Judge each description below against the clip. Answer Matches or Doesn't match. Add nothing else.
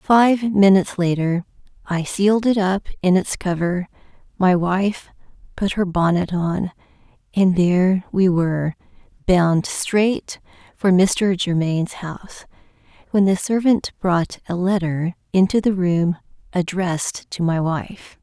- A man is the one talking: Doesn't match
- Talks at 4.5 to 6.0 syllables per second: Doesn't match